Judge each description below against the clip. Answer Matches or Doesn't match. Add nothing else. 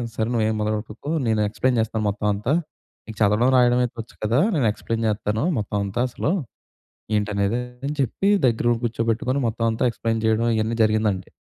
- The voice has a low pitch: Matches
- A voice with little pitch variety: Matches